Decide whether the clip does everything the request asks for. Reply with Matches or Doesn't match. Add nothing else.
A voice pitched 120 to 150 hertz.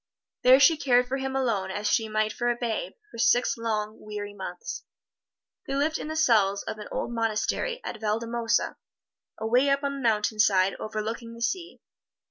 Doesn't match